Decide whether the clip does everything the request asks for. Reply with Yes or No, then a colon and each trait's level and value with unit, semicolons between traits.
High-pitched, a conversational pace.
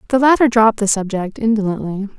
Yes: high, 215 Hz; average, 165 wpm